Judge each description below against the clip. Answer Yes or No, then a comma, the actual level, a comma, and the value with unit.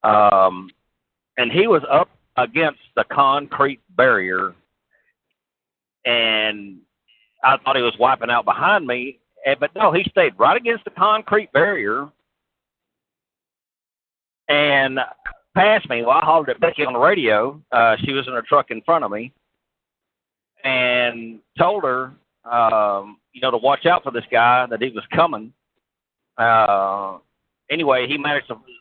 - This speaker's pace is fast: No, average, 145 wpm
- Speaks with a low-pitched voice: Yes, low, 130 Hz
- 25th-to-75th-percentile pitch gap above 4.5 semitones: Yes, average, 5.1 semitones